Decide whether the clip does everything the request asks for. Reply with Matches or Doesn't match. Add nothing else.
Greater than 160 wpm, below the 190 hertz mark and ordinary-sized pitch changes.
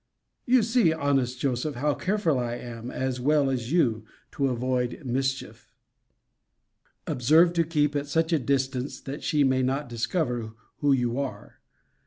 Doesn't match